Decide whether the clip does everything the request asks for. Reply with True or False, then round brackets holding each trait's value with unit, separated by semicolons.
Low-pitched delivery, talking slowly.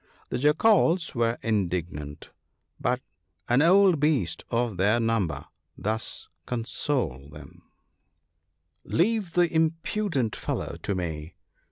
True (120 Hz; 115 wpm)